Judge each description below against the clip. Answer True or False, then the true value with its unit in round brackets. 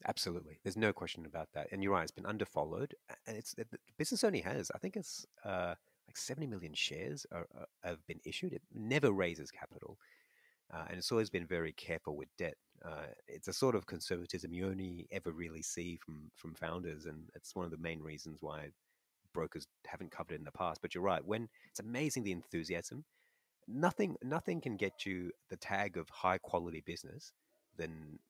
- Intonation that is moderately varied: True (3.0 semitones)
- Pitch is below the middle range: True (85 Hz)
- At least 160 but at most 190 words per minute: False (200 wpm)